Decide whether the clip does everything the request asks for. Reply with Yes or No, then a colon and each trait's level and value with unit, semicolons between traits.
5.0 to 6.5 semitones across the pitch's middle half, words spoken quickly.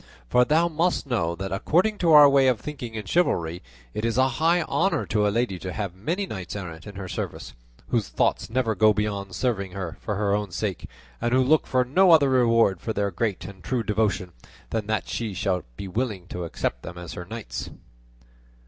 Yes: average, 5.3 semitones; fast, 210 wpm